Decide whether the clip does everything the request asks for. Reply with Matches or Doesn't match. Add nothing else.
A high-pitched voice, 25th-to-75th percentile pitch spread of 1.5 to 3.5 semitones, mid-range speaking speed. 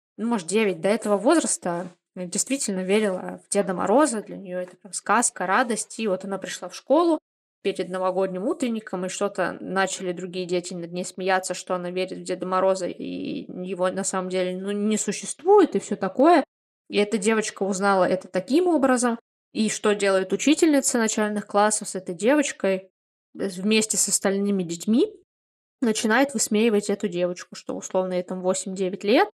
Doesn't match